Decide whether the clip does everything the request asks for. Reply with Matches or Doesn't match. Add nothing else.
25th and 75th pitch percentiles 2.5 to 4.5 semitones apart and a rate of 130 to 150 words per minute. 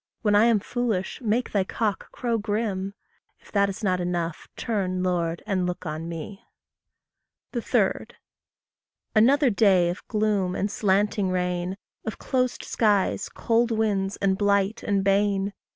Matches